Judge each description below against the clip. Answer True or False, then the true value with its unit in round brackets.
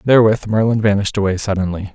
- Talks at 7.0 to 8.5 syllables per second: True (7.1 syllables/s)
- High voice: False (100 Hz)